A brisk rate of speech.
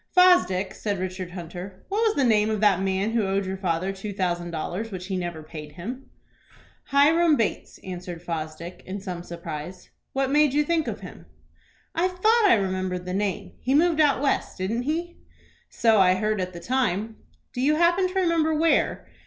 No: average, 185 wpm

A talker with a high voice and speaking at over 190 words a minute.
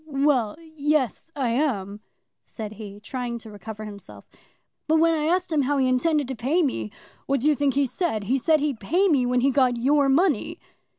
Yes: very high, 270 Hz; average, 200 wpm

